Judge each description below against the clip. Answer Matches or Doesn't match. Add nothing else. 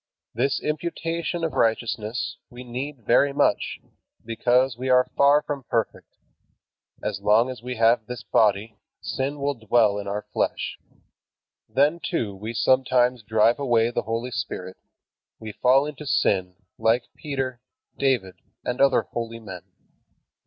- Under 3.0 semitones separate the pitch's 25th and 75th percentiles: Doesn't match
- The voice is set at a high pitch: Doesn't match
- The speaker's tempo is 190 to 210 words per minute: Doesn't match